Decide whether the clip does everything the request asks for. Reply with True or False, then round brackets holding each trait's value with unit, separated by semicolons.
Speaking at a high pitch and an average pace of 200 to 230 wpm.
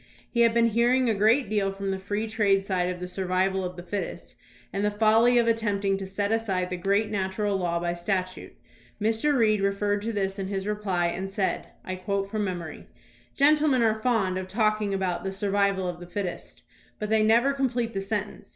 True (200 Hz; 205 wpm)